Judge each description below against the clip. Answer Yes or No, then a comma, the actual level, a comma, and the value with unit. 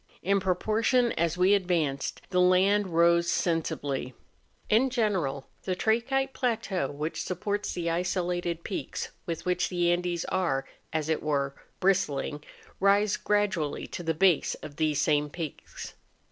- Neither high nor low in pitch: Yes, medium, 180 Hz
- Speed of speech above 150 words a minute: No, slow, 135 wpm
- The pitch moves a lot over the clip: No, average, 3.9 semitones